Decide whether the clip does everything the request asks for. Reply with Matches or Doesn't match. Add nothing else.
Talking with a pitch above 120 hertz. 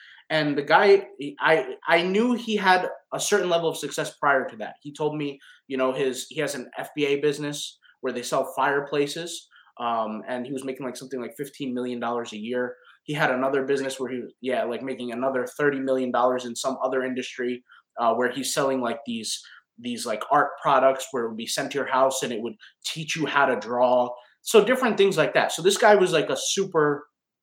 Matches